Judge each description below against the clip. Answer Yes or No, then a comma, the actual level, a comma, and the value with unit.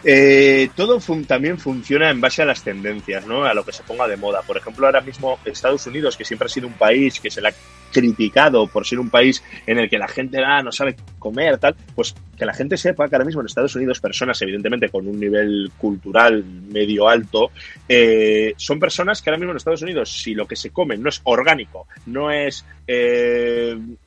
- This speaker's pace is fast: Yes, fast, 220 wpm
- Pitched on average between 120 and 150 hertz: Yes, low, 125 Hz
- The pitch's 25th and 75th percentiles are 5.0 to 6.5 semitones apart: Yes, average, 5.3 semitones